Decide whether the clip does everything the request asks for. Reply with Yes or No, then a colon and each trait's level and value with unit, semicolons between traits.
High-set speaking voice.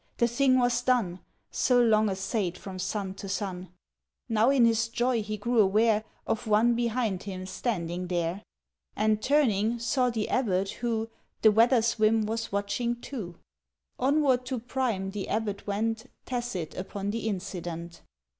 Yes: high, 220 Hz